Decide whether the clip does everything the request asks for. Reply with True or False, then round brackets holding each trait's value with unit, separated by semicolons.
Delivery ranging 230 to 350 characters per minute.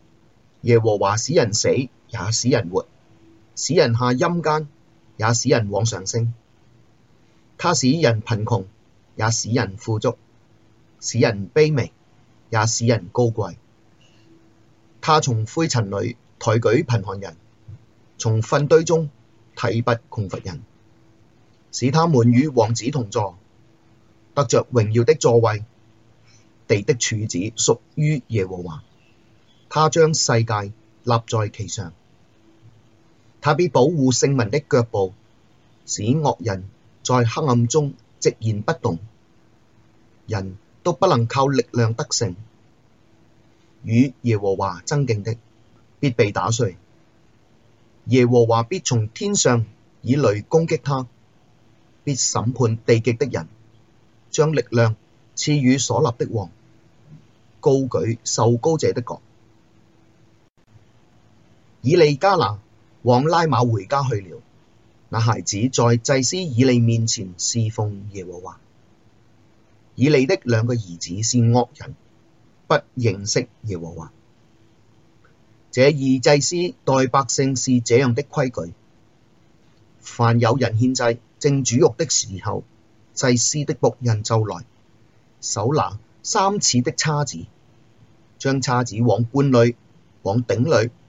False (170 characters per minute)